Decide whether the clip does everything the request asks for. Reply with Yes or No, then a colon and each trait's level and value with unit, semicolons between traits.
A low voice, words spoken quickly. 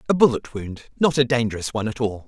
Yes: low, 120 Hz; fast, 210 wpm